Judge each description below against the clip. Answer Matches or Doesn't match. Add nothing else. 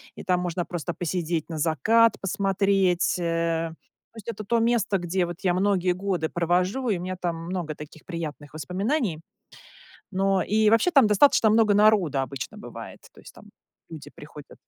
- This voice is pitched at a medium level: Matches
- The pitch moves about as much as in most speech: Matches